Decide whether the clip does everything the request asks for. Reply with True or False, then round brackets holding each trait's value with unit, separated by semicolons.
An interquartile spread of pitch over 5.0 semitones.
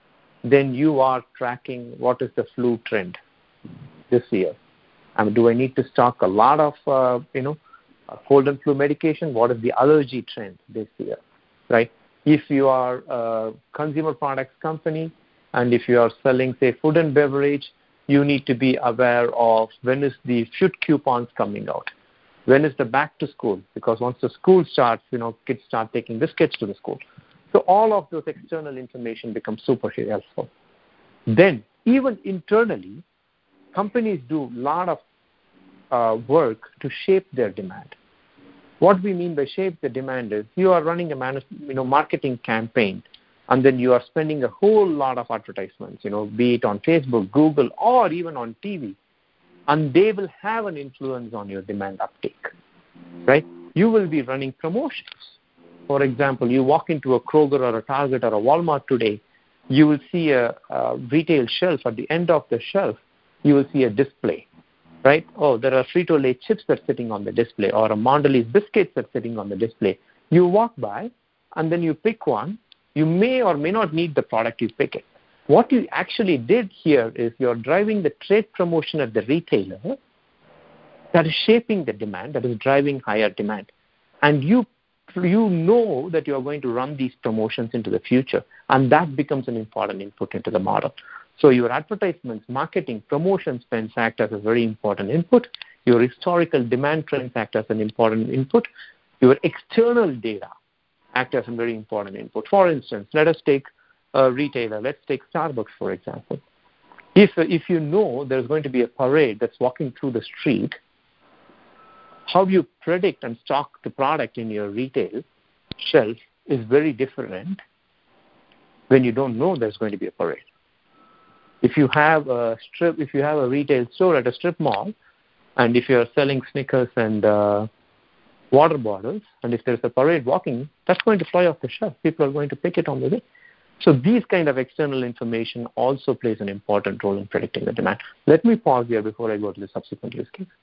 True (5.6 semitones)